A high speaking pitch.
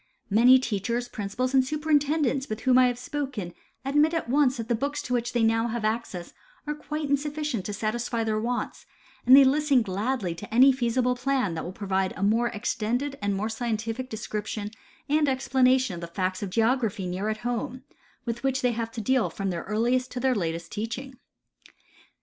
Yes: high, 240 Hz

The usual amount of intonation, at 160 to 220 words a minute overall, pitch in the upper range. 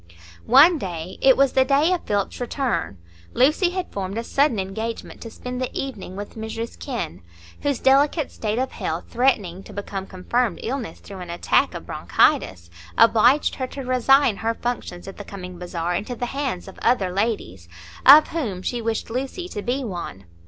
No: wide, 5.9 semitones; average, 175 wpm; high, 230 Hz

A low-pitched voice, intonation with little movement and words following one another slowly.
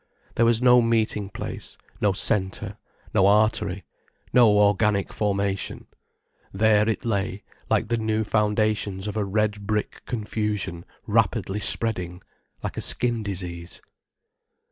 Yes: low, 105 Hz; narrow, 2.0 semitones; slow, 120 wpm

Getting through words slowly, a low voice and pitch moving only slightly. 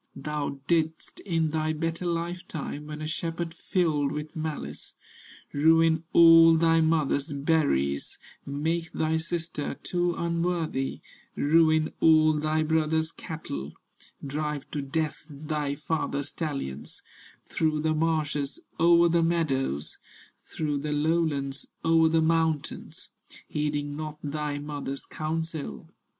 No: slow, 115 wpm; medium, 155 Hz; narrow, 2.0 semitones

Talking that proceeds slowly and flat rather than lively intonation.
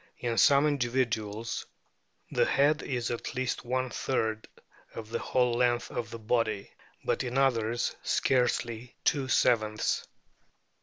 Yes: slow, 125 wpm; narrow, 2.3 semitones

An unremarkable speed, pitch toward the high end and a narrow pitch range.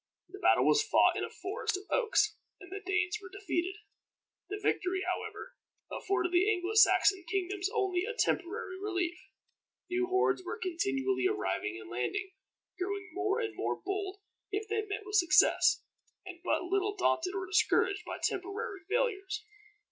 Yes: average, 155 wpm; very high, 385 Hz; narrow, 2.1 semitones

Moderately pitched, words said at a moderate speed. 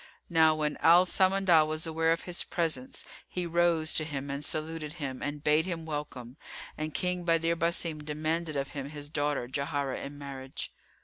Yes: medium, 155 Hz; average, 175 wpm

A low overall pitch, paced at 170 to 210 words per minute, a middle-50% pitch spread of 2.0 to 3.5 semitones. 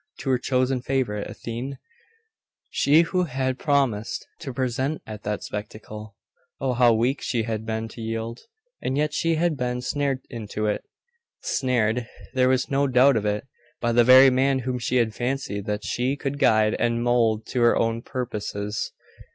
Yes: low, 125 Hz; average, 175 wpm; average, 3.2 semitones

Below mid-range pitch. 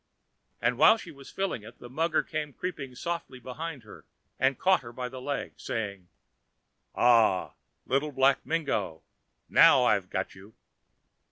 Yes: low, 130 Hz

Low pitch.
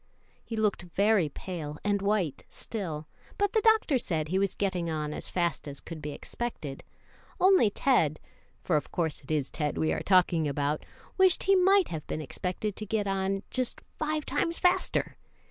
No: high, 190 Hz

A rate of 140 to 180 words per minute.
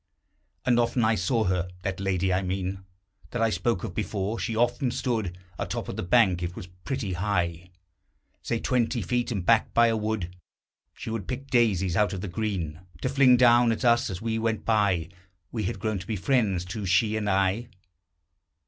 No: average, 195 wpm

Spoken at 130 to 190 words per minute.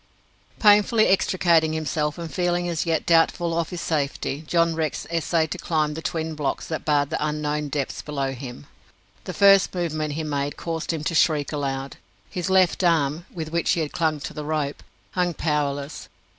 Yes: average, 175 wpm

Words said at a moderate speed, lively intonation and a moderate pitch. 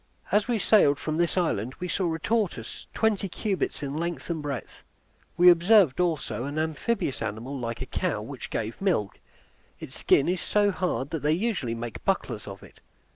Yes: average, 180 wpm; wide, 6.0 semitones; medium, 160 Hz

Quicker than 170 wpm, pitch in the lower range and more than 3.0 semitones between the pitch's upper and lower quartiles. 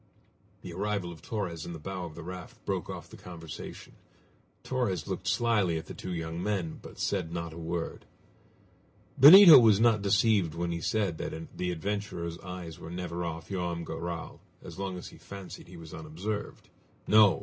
Yes: average, 180 wpm; very low, 90 Hz; average, 3.4 semitones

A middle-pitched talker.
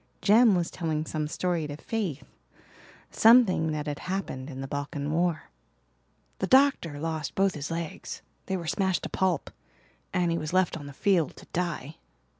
Yes: medium, 165 Hz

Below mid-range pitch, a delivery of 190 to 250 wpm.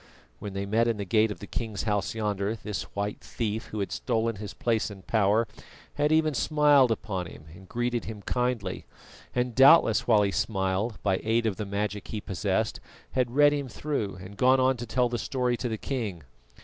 Yes: low, 110 Hz; average, 200 wpm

